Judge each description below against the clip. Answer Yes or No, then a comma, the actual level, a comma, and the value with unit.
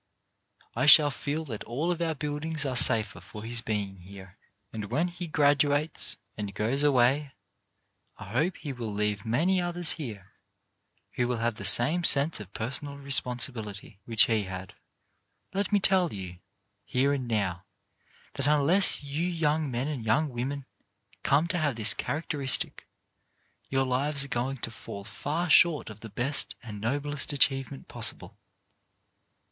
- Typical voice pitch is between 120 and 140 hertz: Yes, low, 135 Hz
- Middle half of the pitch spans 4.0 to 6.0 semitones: Yes, average, 5.3 semitones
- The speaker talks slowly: No, average, 155 wpm